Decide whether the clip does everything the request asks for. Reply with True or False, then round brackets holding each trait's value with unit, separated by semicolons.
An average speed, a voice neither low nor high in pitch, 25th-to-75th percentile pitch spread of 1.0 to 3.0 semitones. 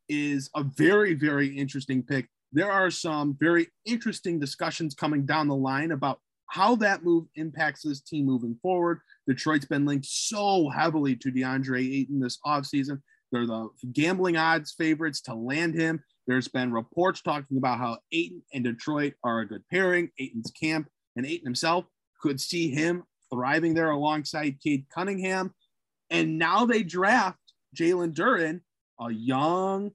False (155 wpm; 150 Hz; 4.1 semitones)